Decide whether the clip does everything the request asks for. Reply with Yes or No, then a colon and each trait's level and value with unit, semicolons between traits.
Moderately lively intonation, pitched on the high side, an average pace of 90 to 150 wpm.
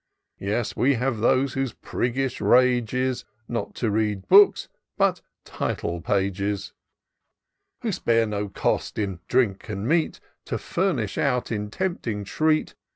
No: average, 4.1 semitones; low, 115 Hz; average, 140 wpm